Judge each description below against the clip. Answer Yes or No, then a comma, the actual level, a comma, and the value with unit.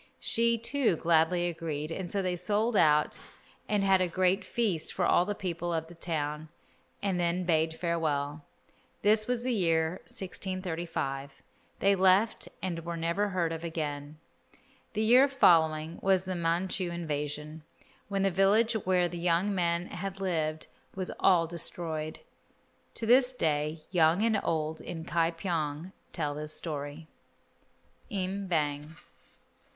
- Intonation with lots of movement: No, average, 3.3 semitones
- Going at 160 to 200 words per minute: No, average, 145 wpm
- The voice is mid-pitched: Yes, medium, 170 Hz